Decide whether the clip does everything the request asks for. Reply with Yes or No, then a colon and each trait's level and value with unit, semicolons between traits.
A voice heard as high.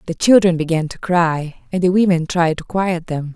No: medium, 170 Hz